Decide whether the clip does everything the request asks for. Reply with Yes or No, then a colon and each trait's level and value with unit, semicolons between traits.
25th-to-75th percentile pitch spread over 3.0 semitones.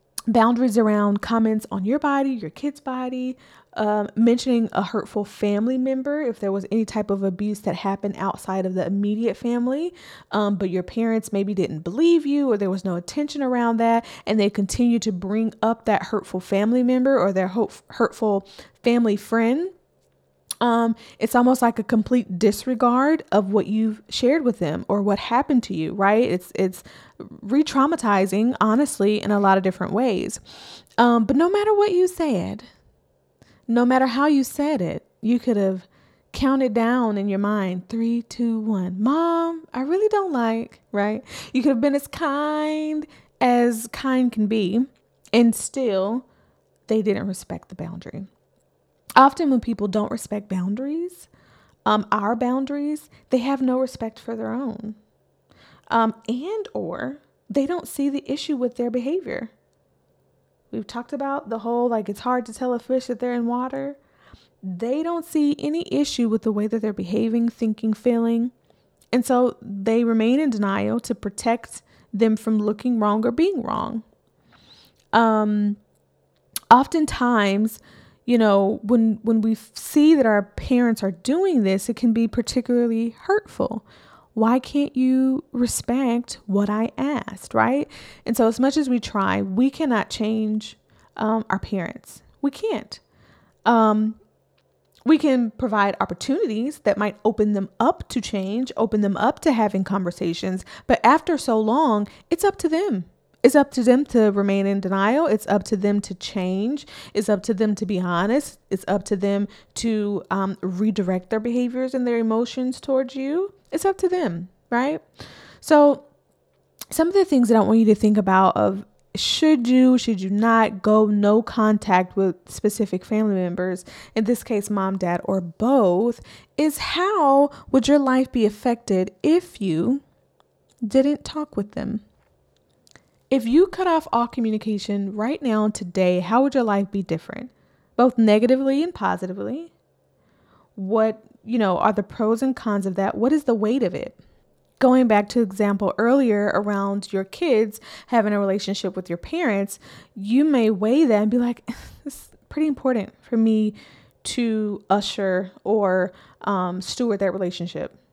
Yes: average, 4.1 semitones